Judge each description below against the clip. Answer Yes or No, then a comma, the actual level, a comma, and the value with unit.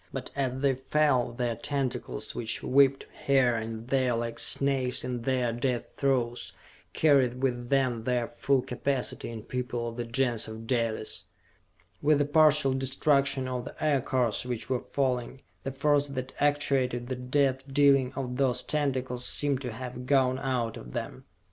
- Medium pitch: No, low, 130 Hz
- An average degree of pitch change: No, narrow, 2.1 semitones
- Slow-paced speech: No, average, 160 wpm